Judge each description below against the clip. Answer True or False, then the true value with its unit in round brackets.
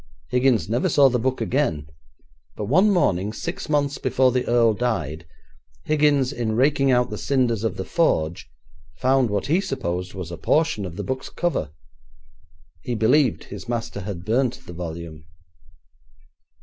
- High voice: False (120 Hz)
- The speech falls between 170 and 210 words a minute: False (155 wpm)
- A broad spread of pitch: True (5.9 semitones)